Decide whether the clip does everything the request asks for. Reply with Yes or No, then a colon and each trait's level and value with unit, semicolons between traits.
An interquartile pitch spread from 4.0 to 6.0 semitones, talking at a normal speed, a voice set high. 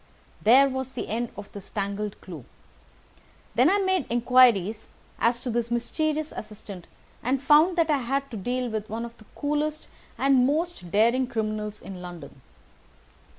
Yes: average, 4.6 semitones; average, 155 wpm; high, 240 Hz